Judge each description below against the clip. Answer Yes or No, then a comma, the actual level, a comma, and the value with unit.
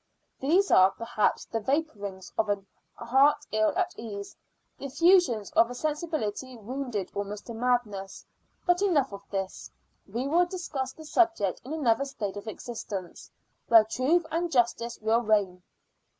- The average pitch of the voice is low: No, high, 235 Hz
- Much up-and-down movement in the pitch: Yes, wide, 6.2 semitones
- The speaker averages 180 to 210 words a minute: No, average, 150 wpm